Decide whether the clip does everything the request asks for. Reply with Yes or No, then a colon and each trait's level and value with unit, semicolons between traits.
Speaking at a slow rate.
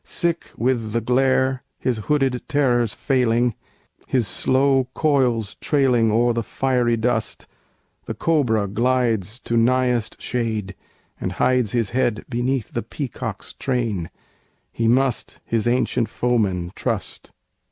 Yes: slow, 120 wpm